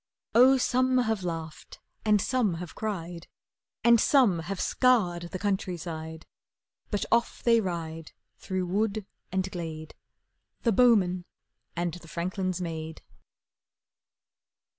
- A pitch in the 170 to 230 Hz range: Yes, medium, 185 Hz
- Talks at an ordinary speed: No, slow, 115 wpm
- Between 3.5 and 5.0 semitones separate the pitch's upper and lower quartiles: Yes, average, 4.7 semitones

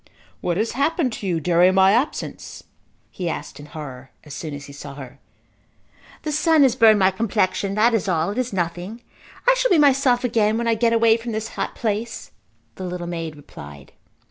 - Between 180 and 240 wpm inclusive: Yes, average, 195 wpm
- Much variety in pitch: Yes, wide, 5.8 semitones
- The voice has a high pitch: Yes, high, 205 Hz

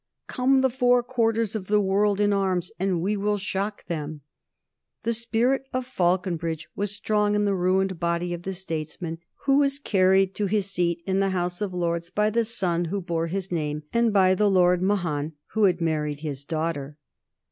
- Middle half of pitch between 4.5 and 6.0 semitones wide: No, average, 3.5 semitones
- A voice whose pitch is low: No, high, 190 Hz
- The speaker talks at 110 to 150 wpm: No, average, 190 wpm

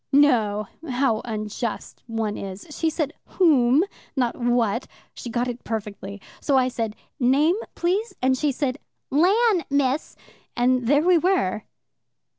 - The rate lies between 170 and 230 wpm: No, slow, 135 wpm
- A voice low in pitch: No, very high, 255 Hz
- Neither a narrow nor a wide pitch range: Yes, average, 4.7 semitones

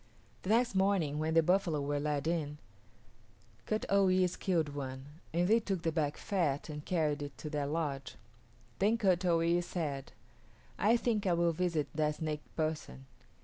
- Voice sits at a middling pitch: Yes, medium, 165 Hz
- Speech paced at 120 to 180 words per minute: Yes, average, 175 wpm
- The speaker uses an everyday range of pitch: Yes, average, 3.8 semitones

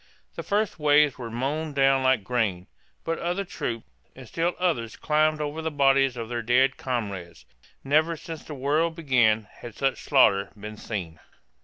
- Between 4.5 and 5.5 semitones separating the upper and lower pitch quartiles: Yes, average, 5.0 semitones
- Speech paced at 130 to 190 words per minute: Yes, average, 165 wpm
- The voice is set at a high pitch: No, low, 135 Hz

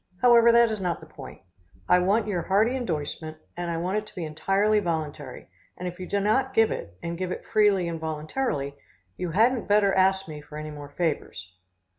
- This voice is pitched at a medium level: Yes, medium, 180 Hz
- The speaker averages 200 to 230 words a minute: Yes, fast, 205 wpm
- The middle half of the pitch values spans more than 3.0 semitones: Yes, average, 5.2 semitones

